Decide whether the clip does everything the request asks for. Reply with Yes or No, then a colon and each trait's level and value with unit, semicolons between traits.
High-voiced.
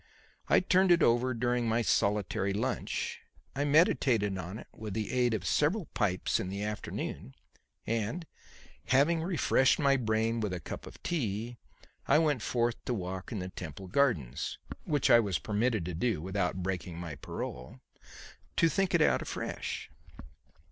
No: low, 115 Hz